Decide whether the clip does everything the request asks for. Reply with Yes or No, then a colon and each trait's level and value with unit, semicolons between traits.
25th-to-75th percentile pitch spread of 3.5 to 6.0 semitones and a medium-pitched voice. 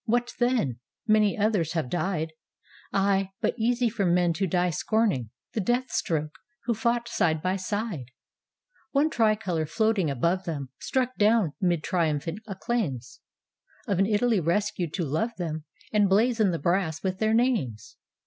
No: average, 5.3 semitones; high, 195 Hz